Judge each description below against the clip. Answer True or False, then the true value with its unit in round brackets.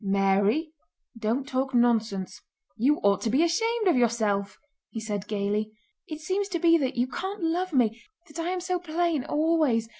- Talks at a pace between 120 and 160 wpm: False (175 wpm)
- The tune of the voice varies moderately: False (7.4 semitones)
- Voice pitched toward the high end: True (260 Hz)